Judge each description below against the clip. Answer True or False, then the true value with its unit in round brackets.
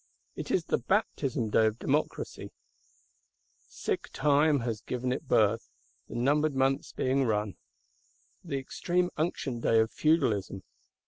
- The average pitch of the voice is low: True (130 Hz)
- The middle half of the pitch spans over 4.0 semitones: True (4.7 semitones)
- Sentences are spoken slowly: True (130 wpm)